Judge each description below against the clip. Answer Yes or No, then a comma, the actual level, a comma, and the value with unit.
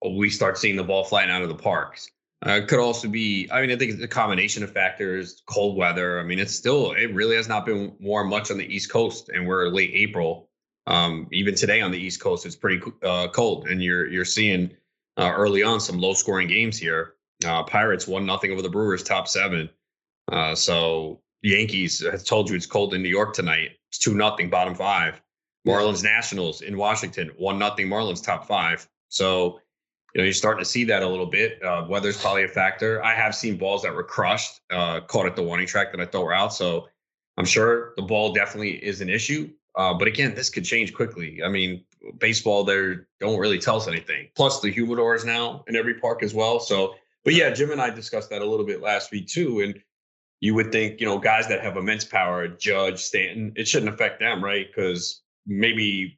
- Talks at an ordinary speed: No, fast, 220 wpm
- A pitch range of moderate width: Yes, average, 3.1 semitones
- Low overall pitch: Yes, low, 100 Hz